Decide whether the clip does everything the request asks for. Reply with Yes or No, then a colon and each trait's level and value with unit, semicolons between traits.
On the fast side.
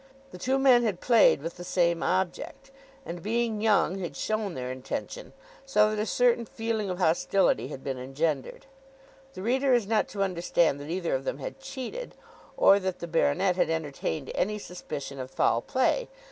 No: average, 180 wpm